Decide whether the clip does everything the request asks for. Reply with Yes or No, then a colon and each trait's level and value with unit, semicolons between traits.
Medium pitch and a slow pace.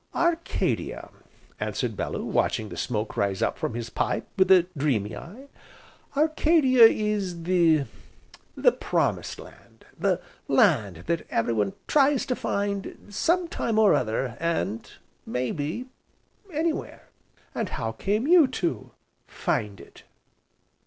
Yes: medium, 180 Hz; slow, 120 wpm